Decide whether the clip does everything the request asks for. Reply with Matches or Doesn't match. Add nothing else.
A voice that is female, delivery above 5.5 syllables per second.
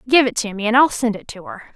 Matches